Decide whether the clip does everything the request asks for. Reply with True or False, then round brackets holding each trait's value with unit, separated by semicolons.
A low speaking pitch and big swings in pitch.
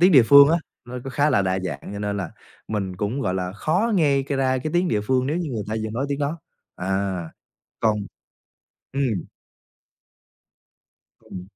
True (125 Hz; 6.2 semitones)